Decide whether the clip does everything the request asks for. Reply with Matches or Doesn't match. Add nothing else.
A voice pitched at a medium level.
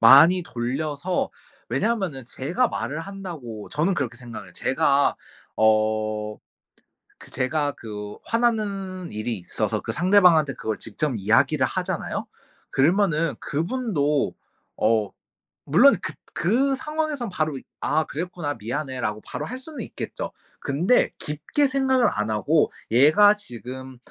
Matches